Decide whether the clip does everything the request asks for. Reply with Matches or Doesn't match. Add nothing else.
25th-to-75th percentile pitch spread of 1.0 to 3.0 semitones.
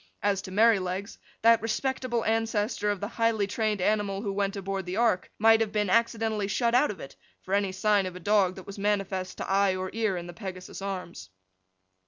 Matches